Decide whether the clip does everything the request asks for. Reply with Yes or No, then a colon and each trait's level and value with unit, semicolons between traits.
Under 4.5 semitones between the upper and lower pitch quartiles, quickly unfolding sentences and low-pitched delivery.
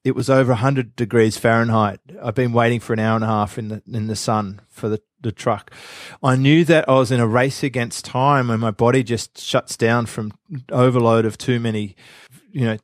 Yes: average, 2.9 semitones; fast, 220 wpm; low, 120 Hz